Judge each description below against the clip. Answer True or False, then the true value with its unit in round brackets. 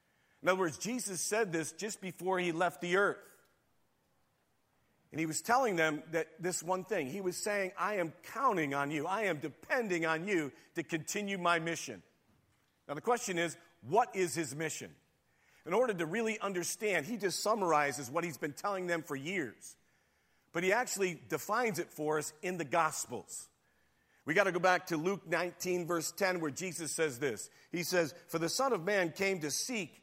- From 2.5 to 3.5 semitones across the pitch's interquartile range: True (3.2 semitones)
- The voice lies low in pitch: False (175 Hz)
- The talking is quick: False (190 wpm)